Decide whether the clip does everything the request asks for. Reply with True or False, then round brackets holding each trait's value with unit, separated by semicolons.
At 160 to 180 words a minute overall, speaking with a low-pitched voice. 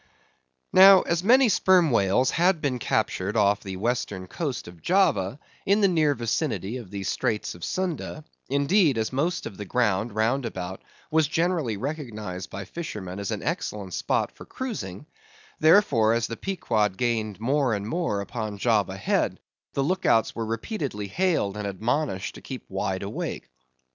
True (165 wpm; 115 Hz)